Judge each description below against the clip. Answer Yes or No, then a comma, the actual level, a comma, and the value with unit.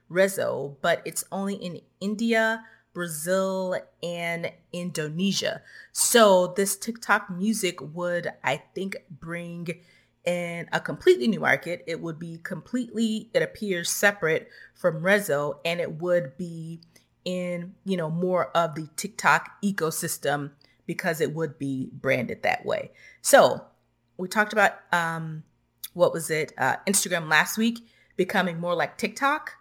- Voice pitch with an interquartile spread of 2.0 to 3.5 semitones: Yes, average, 3.1 semitones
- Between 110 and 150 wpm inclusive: Yes, slow, 135 wpm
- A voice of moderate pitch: Yes, medium, 175 Hz